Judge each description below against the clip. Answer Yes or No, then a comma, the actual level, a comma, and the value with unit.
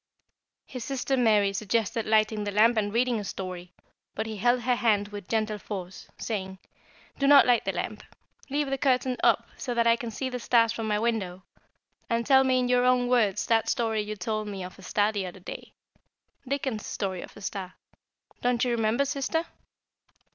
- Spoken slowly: No, average, 195 wpm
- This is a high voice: Yes, high, 225 Hz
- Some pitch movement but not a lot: Yes, average, 3.3 semitones